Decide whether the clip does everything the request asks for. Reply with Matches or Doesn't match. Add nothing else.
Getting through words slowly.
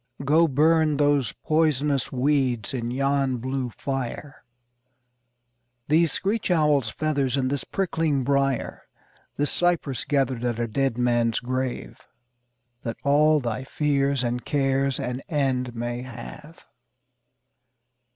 Matches